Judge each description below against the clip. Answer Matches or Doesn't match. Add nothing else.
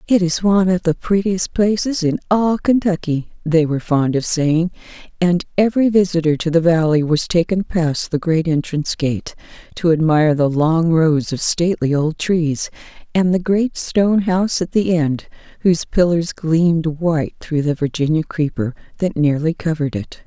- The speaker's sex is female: Matches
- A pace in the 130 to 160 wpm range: Doesn't match